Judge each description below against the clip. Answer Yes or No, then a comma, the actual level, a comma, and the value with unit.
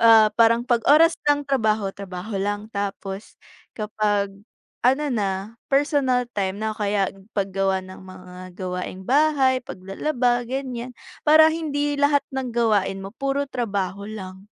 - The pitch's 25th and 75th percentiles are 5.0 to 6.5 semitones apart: Yes, wide, 5.4 semitones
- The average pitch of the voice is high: Yes, high, 220 Hz